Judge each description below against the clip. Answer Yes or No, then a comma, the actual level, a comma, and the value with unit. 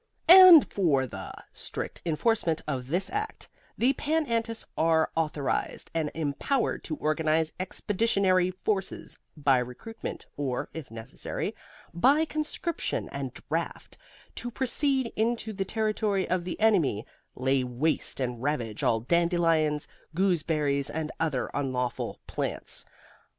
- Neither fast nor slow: No, slow, 120 wpm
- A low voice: No, medium, 165 Hz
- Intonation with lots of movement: Yes, wide, 7.5 semitones